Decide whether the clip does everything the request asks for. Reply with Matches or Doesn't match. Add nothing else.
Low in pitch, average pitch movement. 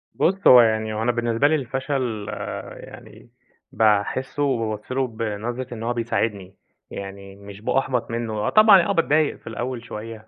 Matches